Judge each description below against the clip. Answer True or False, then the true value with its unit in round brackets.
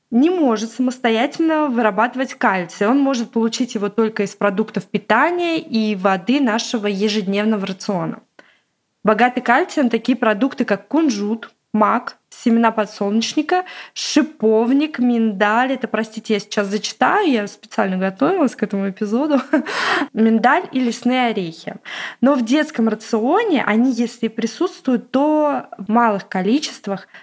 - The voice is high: True (230 Hz)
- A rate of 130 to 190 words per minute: False (120 wpm)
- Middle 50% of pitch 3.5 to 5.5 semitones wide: True (4.0 semitones)